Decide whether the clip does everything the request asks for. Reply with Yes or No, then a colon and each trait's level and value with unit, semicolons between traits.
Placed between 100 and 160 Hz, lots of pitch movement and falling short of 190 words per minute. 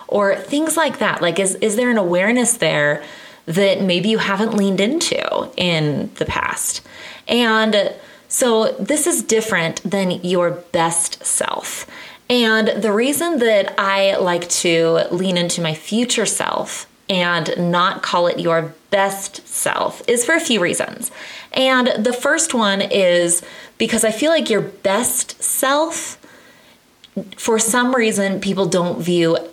No: high, 200 Hz; wide, 5.7 semitones; average, 145 wpm